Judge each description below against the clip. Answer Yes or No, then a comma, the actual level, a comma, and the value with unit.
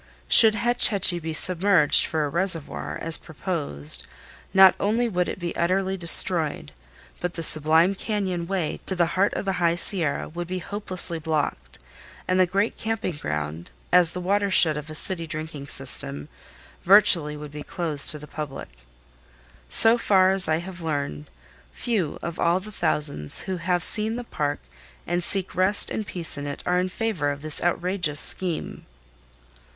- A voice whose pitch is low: No, medium, 175 Hz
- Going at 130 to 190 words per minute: Yes, average, 165 wpm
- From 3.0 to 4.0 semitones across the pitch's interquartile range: Yes, average, 3.7 semitones